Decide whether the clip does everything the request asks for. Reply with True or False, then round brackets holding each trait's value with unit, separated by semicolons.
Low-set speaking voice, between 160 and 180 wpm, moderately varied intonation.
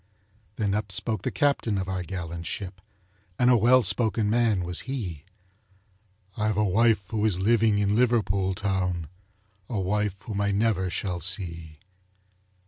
False (100 Hz; 150 wpm; 3.1 semitones)